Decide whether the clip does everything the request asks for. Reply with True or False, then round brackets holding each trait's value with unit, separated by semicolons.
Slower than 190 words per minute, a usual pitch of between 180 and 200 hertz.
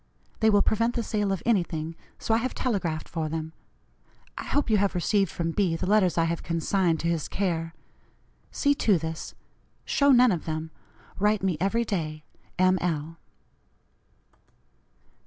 True (160 wpm; 185 Hz)